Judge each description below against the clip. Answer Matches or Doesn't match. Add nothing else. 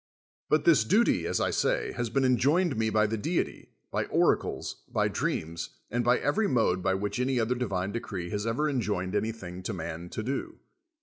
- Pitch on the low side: Matches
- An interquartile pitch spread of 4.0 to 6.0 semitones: Matches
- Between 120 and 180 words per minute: Doesn't match